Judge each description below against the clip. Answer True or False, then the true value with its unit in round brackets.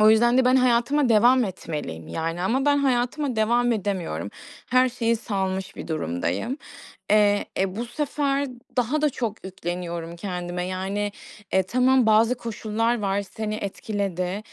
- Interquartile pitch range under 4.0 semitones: False (4.7 semitones)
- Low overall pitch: False (215 Hz)